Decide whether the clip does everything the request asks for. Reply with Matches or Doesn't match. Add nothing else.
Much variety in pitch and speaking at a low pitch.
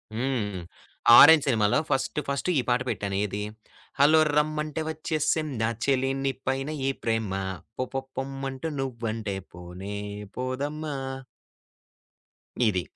Doesn't match